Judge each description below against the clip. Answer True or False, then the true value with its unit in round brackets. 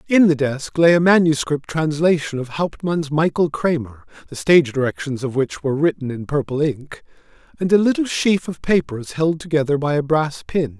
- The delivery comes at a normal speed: True (185 wpm)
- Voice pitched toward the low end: False (155 Hz)